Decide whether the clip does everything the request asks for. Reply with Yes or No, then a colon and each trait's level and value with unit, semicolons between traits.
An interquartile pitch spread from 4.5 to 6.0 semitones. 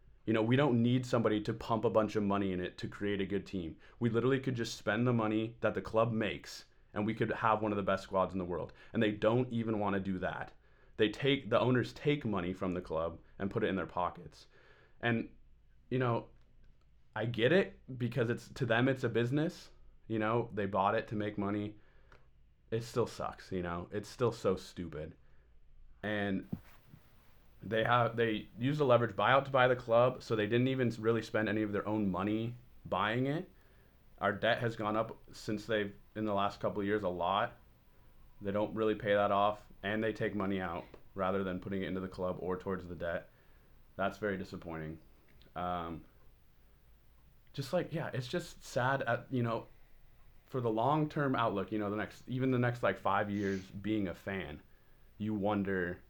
No: average, 3.2 semitones